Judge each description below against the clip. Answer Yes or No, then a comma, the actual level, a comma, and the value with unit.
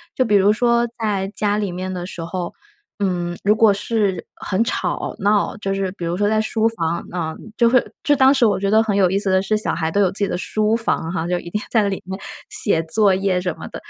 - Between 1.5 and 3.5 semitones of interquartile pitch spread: Yes, average, 3.0 semitones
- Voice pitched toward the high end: Yes, high, 200 Hz